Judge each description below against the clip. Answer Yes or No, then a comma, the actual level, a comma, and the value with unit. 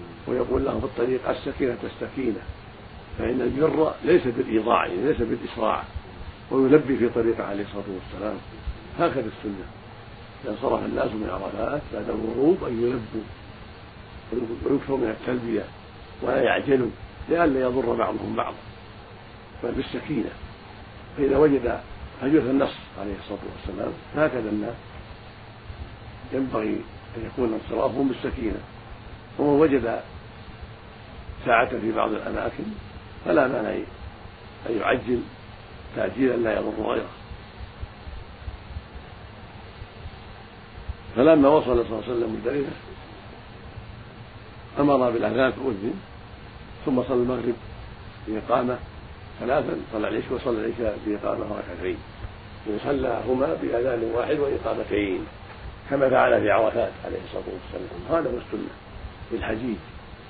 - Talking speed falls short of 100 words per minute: No, average, 105 wpm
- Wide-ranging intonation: No, average, 2.8 semitones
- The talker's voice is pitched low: Yes, low, 110 Hz